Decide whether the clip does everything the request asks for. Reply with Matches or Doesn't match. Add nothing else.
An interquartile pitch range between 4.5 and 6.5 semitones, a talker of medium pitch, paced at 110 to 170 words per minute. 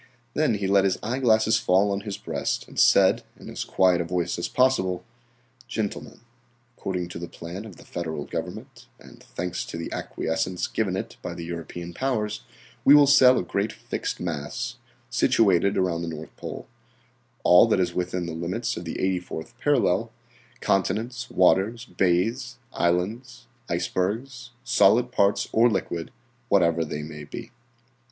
Doesn't match